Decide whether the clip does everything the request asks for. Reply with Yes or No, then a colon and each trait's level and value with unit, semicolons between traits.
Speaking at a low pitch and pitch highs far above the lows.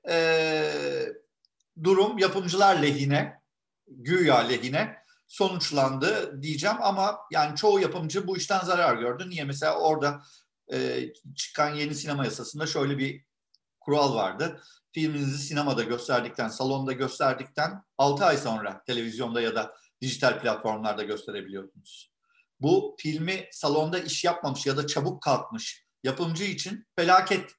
No: medium, 155 Hz; wide, 5.8 semitones